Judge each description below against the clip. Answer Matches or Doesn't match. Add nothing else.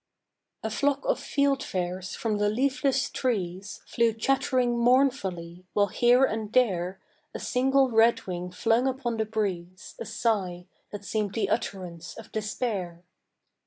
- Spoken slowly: Matches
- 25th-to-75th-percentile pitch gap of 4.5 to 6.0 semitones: Matches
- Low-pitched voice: Doesn't match